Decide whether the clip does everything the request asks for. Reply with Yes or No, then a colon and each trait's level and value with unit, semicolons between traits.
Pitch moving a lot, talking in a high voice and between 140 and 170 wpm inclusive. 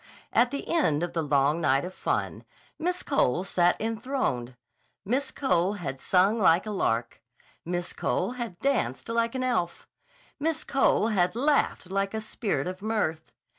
Yes: wide, 6.3 semitones; high, 195 Hz; average, 160 wpm